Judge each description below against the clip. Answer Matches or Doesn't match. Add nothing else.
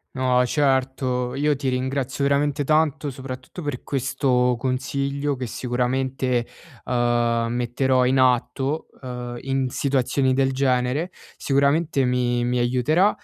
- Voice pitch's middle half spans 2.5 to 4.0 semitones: Doesn't match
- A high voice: Doesn't match